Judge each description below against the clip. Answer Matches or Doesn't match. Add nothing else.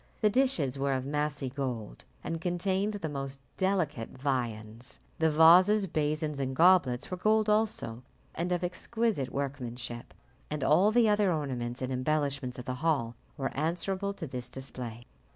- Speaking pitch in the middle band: Matches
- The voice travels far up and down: Matches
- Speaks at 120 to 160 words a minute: Matches